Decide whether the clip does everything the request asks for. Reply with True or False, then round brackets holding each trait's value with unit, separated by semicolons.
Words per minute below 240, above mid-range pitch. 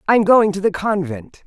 True (205 wpm; 215 Hz)